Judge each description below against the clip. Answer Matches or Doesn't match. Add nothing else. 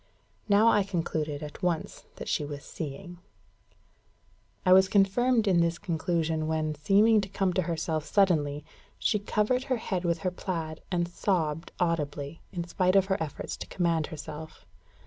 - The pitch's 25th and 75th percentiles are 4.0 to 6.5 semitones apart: Doesn't match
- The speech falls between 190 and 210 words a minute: Doesn't match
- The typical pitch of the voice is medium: Matches